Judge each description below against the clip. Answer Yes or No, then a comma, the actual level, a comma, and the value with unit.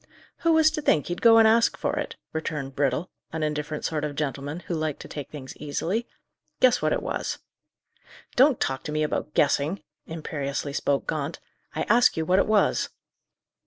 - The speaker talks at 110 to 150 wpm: No, average, 185 wpm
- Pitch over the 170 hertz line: No, medium, 155 Hz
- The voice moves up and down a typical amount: No, wide, 6.4 semitones